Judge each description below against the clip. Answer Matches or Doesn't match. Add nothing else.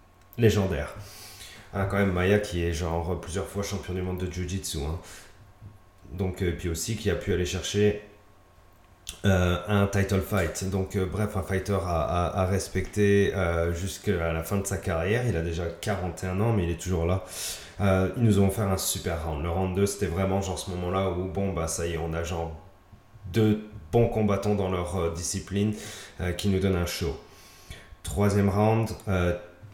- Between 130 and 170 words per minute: Doesn't match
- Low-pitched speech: Matches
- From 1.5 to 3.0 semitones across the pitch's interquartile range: Matches